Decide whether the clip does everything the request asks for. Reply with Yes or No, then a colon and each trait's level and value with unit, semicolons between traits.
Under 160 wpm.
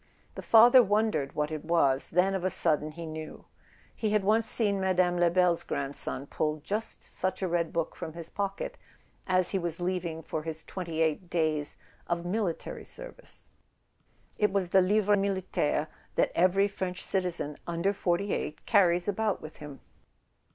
No: average, 165 wpm